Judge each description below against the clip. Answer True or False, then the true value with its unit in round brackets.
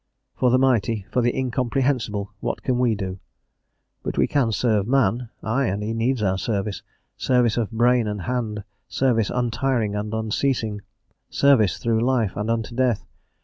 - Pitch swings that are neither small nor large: True (3.0 semitones)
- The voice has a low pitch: True (115 Hz)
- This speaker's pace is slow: False (160 wpm)